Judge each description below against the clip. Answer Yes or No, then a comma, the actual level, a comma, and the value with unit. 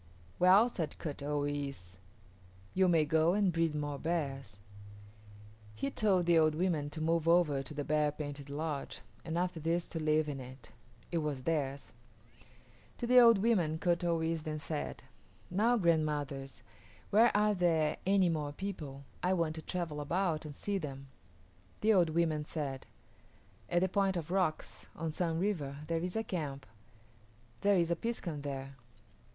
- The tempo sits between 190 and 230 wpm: No, average, 165 wpm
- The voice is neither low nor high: Yes, medium, 160 Hz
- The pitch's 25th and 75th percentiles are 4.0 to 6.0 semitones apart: No, average, 3.5 semitones